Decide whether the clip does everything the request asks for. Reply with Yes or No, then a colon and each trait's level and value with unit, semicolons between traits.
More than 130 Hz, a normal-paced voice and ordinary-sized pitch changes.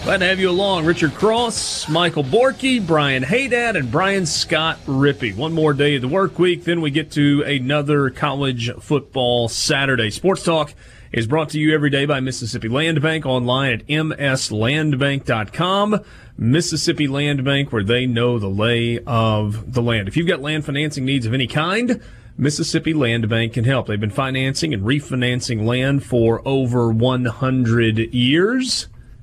Yes: medium, 140 Hz; average, 165 wpm; average, 4.6 semitones